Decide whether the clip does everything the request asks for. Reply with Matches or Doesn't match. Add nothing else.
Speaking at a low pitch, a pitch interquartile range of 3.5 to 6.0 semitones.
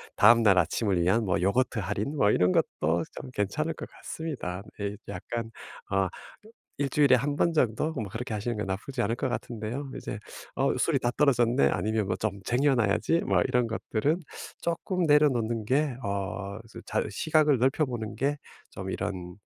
Matches